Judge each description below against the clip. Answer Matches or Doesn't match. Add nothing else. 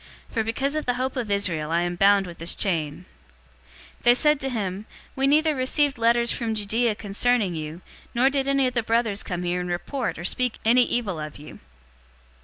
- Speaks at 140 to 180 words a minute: Doesn't match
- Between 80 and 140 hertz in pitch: Doesn't match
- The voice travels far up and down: Matches